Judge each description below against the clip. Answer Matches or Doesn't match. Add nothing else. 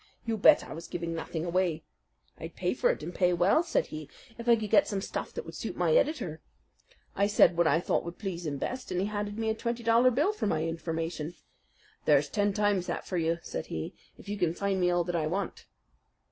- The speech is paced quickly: Matches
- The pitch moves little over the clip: Doesn't match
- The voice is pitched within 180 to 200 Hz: Matches